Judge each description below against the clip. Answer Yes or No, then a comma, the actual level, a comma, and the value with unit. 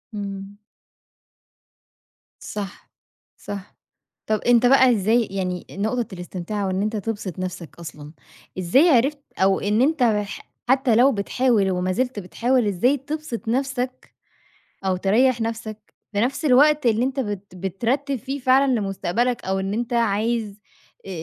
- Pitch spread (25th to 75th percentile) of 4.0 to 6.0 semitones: Yes, average, 4.6 semitones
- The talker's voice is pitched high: Yes, high, 220 Hz